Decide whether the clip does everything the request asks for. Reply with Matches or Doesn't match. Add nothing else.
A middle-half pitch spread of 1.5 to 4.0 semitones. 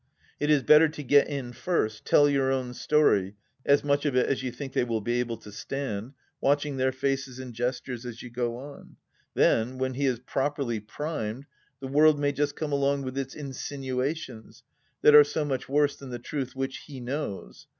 Matches